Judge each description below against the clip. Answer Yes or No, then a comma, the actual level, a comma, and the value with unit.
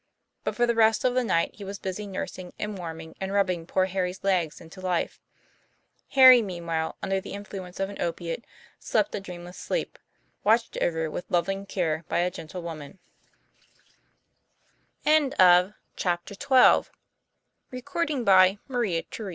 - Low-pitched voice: No, medium, 185 Hz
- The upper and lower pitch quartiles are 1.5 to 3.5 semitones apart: Yes, average, 2.9 semitones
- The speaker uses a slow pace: Yes, slow, 125 wpm